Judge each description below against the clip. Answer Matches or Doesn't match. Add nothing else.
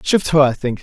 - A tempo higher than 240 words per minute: Matches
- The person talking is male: Matches